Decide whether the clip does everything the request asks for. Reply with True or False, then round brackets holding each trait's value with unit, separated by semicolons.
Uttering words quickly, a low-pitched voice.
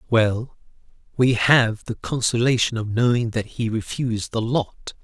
False (145 wpm; 115 Hz)